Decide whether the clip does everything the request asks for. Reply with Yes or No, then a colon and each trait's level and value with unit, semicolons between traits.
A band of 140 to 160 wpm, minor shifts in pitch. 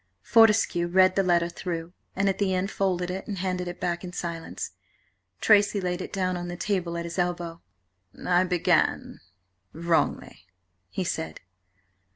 Yes: average, 155 wpm; narrow, 1.8 semitones